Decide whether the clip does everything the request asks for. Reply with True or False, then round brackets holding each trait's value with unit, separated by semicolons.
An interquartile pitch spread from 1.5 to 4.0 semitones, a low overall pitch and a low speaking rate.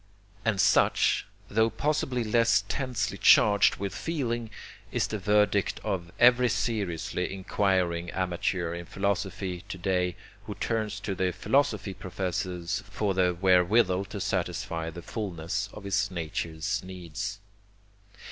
True (3.0 semitones; 95 Hz; 125 wpm)